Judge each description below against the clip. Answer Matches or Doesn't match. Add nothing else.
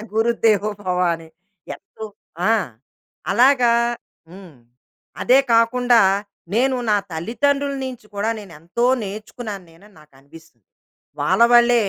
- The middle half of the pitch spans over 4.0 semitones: Matches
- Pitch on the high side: Matches